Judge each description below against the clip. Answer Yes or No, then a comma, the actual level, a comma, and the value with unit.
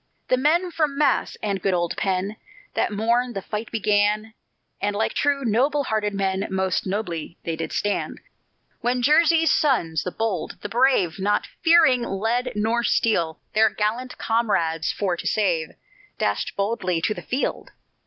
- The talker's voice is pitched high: Yes, high, 215 Hz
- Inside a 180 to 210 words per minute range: No, average, 155 wpm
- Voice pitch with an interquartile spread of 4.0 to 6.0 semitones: Yes, average, 4.6 semitones